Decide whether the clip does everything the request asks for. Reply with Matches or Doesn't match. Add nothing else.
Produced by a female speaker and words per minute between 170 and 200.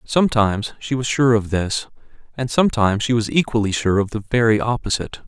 Doesn't match